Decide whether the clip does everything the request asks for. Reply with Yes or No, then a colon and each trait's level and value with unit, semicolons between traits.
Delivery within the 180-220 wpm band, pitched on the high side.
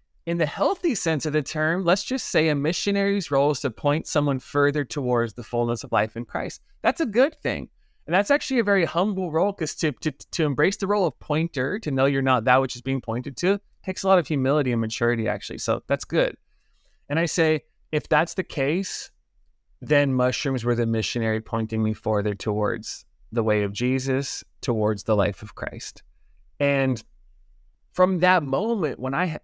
No: average, 200 wpm; medium, 140 Hz